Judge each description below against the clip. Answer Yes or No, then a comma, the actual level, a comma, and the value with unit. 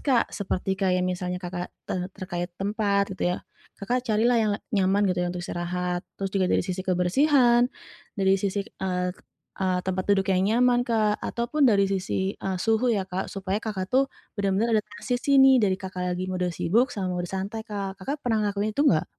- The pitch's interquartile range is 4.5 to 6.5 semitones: No, average, 3.2 semitones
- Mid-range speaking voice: No, high, 195 Hz